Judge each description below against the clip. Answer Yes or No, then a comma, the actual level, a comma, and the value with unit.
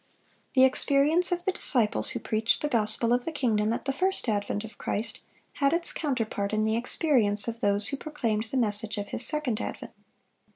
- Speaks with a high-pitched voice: Yes, high, 235 Hz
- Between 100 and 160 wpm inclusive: No, average, 195 wpm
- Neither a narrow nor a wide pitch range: Yes, average, 4.8 semitones